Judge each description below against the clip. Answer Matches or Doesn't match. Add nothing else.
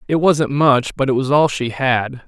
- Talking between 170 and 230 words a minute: Doesn't match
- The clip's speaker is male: Matches